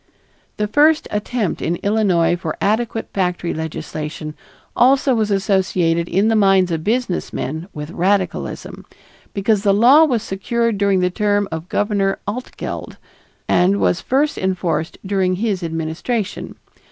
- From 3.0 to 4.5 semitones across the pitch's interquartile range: Yes, average, 3.8 semitones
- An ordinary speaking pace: No, slow, 130 wpm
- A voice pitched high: Yes, high, 195 Hz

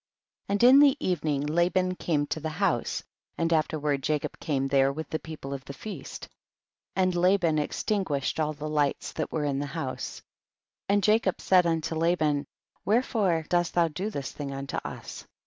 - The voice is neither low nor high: Yes, medium, 160 Hz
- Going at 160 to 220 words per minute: Yes, average, 180 wpm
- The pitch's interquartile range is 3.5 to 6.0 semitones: Yes, average, 4.0 semitones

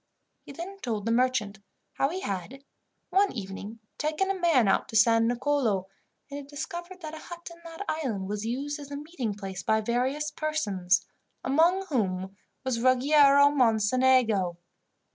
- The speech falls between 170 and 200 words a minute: No, average, 160 wpm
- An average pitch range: No, wide, 6.1 semitones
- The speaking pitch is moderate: No, very high, 260 Hz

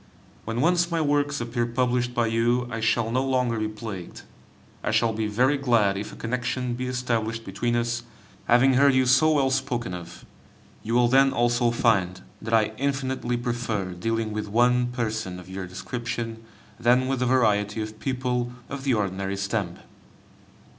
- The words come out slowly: No, average, 170 wpm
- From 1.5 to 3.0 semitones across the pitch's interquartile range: Yes, average, 2.7 semitones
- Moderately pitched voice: No, low, 120 Hz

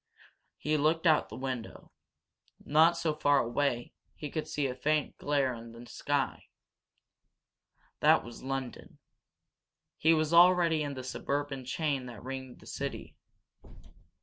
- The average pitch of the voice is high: No, medium, 145 Hz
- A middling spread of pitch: Yes, average, 3.1 semitones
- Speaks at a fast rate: No, average, 145 wpm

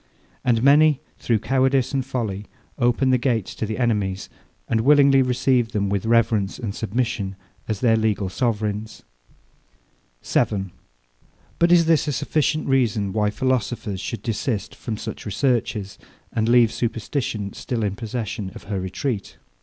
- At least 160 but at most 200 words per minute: No, average, 145 wpm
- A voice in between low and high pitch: No, low, 115 Hz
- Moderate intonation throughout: Yes, average, 3.8 semitones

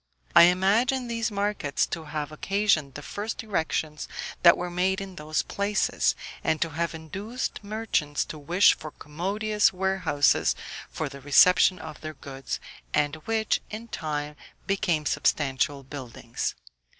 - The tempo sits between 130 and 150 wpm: Yes, average, 140 wpm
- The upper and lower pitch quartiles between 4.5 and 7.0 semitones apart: Yes, average, 5.2 semitones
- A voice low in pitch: No, medium, 170 Hz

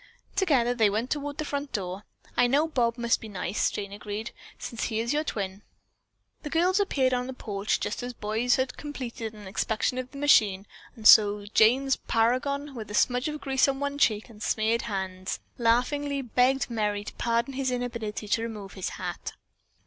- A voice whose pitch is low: No, high, 235 Hz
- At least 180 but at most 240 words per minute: Yes, average, 190 wpm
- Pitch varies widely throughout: No, average, 4.2 semitones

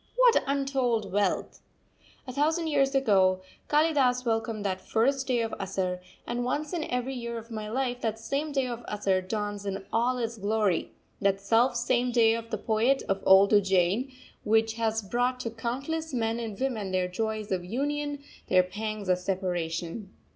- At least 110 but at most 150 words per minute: No, average, 170 wpm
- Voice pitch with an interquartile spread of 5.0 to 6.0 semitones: No, average, 4.3 semitones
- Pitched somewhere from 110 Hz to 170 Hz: No, high, 225 Hz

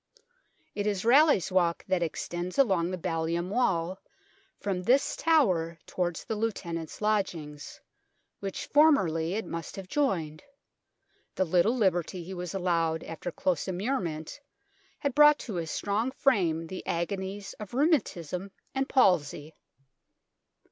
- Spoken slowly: Yes, slow, 125 wpm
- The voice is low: No, medium, 185 Hz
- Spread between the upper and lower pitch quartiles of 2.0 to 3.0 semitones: No, average, 4.4 semitones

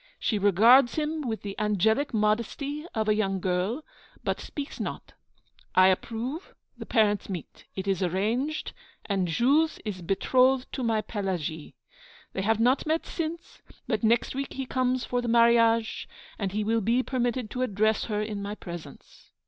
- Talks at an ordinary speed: Yes, average, 165 wpm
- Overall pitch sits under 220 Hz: No, high, 225 Hz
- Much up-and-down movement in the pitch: No, average, 4.2 semitones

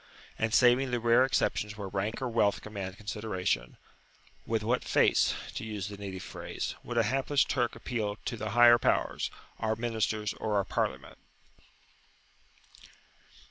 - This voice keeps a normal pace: Yes, average, 145 wpm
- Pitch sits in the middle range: No, low, 110 Hz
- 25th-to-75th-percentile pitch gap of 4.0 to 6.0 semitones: No, narrow, 2.6 semitones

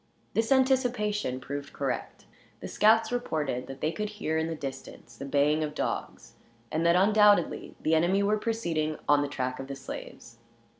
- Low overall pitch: No, medium, 160 Hz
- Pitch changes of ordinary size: No, wide, 6.9 semitones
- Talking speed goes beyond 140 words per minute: Yes, average, 170 wpm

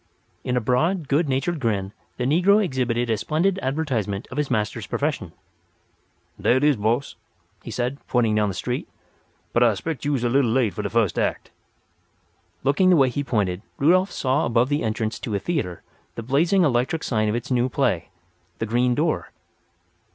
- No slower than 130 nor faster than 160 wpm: No, average, 185 wpm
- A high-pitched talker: No, low, 125 Hz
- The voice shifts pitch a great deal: No, average, 4.7 semitones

